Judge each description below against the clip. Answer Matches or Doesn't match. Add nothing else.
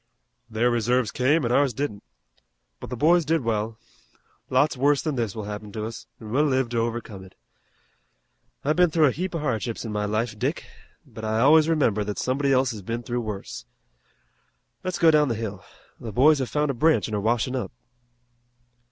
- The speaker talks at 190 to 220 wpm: Matches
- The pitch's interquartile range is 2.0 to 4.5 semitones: Doesn't match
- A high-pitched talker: Doesn't match